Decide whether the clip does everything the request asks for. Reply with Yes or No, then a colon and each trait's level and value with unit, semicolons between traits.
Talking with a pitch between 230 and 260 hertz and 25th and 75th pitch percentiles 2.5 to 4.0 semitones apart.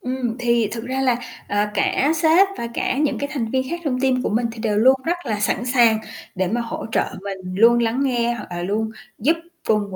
Yes: high, 235 Hz; average, 3.3 semitones